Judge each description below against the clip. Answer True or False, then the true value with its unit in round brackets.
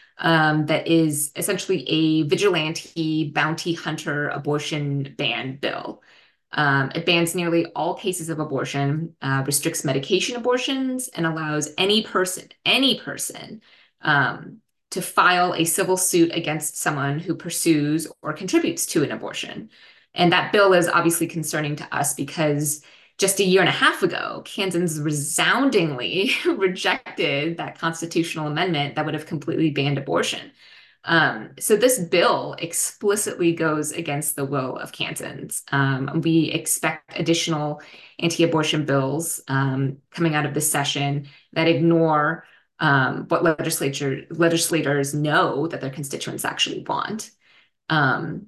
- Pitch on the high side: False (160 Hz)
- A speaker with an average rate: False (130 wpm)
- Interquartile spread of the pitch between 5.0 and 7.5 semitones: False (2.9 semitones)